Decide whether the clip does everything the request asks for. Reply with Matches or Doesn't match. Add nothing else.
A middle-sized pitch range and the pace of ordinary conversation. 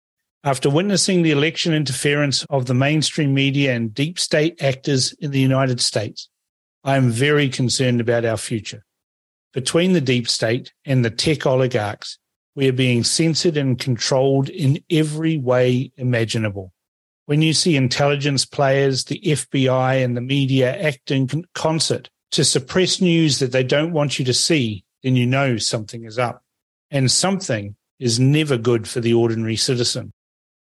Matches